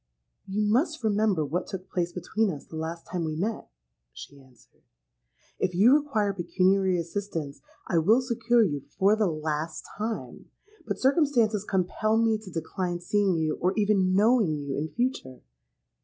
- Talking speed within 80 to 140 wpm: No, average, 155 wpm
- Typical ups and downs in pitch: Yes, average, 4.9 semitones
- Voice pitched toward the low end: No, high, 190 Hz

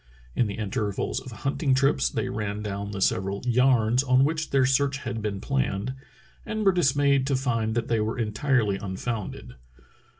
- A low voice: Yes, low, 120 Hz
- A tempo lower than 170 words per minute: No, average, 190 wpm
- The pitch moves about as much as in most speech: Yes, average, 4.6 semitones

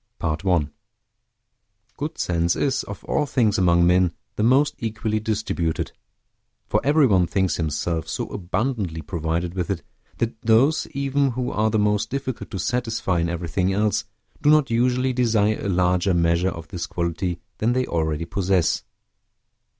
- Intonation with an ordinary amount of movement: No, wide, 5.7 semitones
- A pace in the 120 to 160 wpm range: Yes, average, 155 wpm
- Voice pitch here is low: Yes, low, 100 Hz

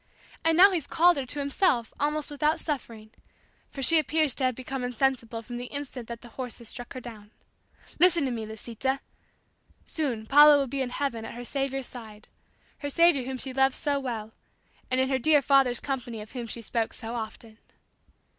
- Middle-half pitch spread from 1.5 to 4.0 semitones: Yes, average, 3.4 semitones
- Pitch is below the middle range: No, very high, 260 Hz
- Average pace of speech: Yes, average, 195 wpm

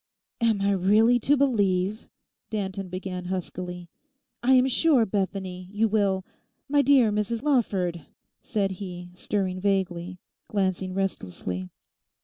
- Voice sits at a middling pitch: No, high, 195 Hz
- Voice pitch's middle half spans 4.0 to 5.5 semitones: No, average, 3.3 semitones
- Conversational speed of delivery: No, slow, 115 wpm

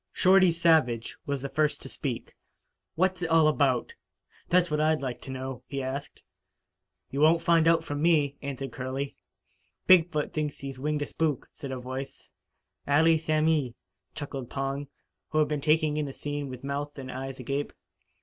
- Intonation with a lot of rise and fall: No, average, 2.8 semitones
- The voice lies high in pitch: No, medium, 145 Hz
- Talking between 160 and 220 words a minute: Yes, average, 175 wpm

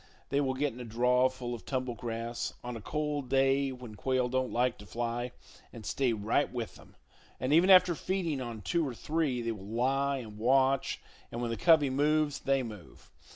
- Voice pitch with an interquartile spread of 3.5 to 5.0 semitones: No, average, 2.9 semitones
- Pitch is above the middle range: No, low, 130 Hz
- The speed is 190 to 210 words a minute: Yes, average, 200 wpm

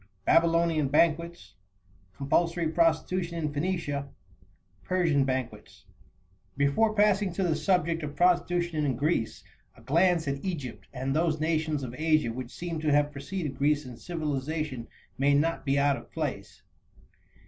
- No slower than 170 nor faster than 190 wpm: No, slow, 135 wpm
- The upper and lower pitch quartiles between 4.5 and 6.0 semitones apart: No, average, 3.4 semitones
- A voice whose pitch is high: No, medium, 155 Hz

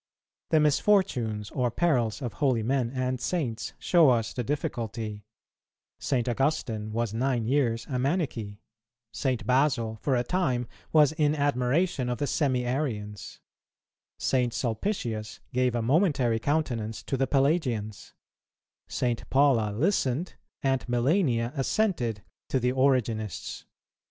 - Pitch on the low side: Yes, low, 125 Hz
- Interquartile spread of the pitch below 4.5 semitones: Yes, average, 3.8 semitones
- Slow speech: Yes, slow, 125 wpm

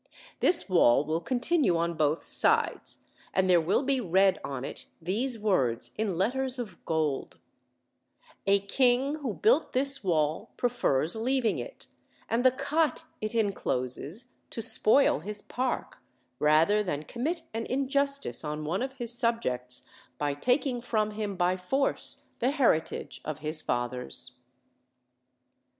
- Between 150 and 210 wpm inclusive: No, average, 140 wpm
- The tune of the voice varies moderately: No, wide, 8.2 semitones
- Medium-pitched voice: No, high, 210 Hz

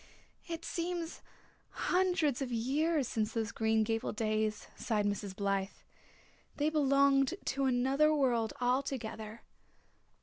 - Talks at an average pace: No, slow, 110 wpm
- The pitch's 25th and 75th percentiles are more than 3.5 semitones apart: Yes, average, 5.1 semitones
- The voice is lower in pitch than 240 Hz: No, very high, 255 Hz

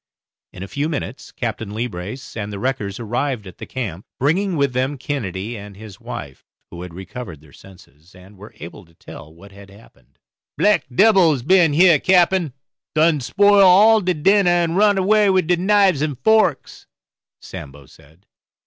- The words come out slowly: No, average, 170 wpm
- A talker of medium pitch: No, low, 130 Hz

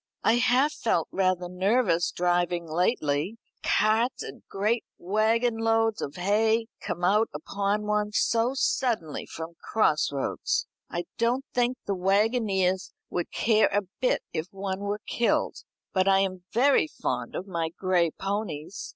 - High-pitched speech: Yes, high, 200 Hz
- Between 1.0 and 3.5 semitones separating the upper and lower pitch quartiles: No, average, 4.1 semitones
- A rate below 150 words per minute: Yes, average, 140 wpm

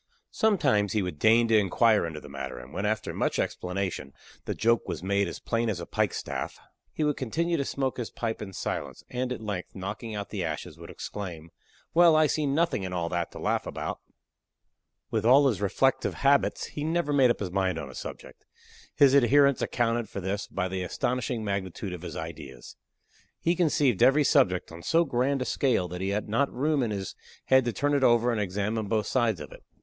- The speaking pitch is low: Yes, low, 110 Hz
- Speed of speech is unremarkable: No, fast, 210 wpm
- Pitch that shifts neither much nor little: No, wide, 6.1 semitones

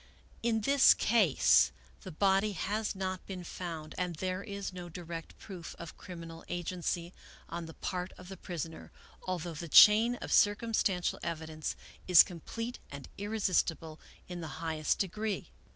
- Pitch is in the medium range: Yes, medium, 180 Hz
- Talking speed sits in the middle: Yes, average, 155 wpm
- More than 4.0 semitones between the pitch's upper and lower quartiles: No, average, 3.3 semitones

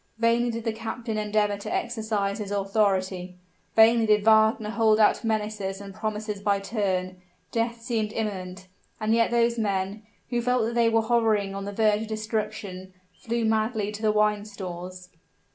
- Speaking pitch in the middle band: No, high, 215 Hz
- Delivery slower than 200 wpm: Yes, average, 165 wpm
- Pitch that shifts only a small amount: Yes, narrow, 2.1 semitones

